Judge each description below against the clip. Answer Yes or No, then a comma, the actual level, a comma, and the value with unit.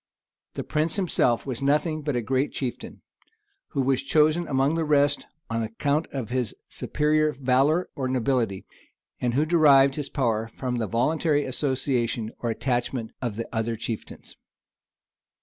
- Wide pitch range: No, average, 3.9 semitones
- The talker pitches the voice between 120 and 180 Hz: Yes, low, 135 Hz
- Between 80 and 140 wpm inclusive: No, average, 155 wpm